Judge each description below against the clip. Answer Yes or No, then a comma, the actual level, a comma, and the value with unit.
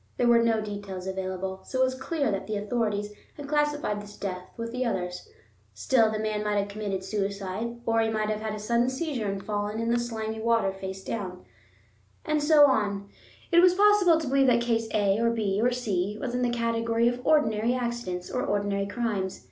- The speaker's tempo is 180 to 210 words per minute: Yes, fast, 205 wpm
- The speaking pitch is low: No, high, 220 Hz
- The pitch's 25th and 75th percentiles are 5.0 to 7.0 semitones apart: No, average, 3.2 semitones